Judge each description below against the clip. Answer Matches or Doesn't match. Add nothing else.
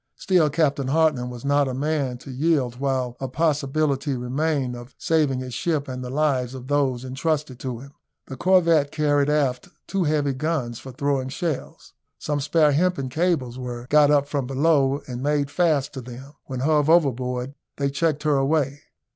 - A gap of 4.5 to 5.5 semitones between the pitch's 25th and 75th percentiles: Doesn't match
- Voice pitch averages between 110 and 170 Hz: Matches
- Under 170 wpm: Doesn't match